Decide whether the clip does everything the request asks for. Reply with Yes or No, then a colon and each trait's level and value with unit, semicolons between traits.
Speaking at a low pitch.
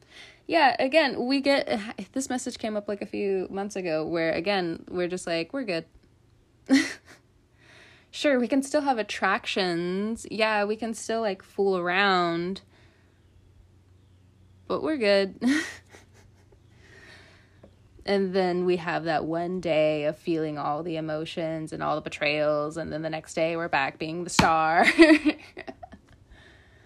No: medium, 170 Hz